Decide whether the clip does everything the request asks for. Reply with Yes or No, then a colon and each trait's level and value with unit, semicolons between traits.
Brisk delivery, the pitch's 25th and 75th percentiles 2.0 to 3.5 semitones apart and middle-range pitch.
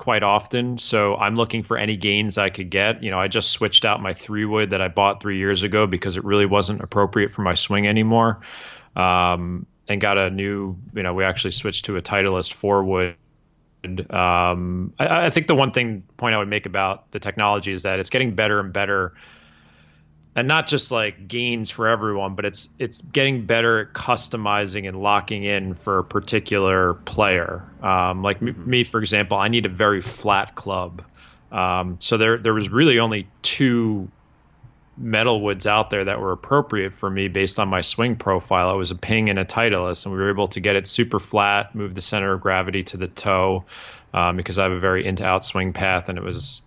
No: fast, 210 wpm; average, 2.8 semitones; low, 100 Hz